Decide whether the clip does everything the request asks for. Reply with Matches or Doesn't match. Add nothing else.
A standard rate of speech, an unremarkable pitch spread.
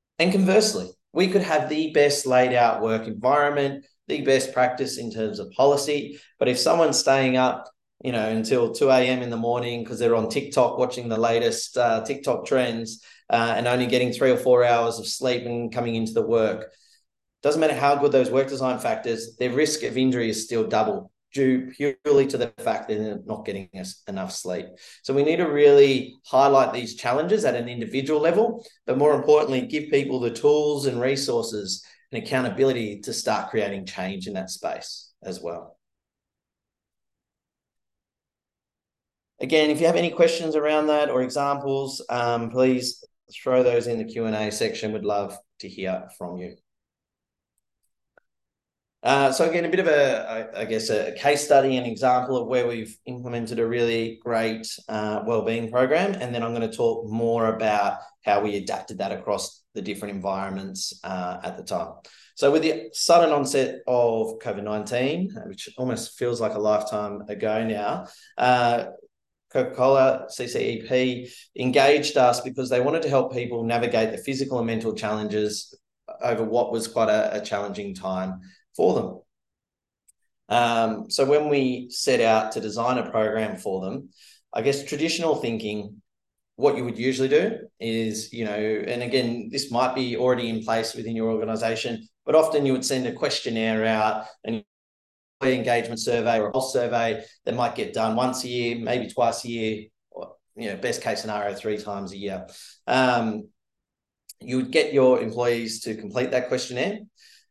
Matches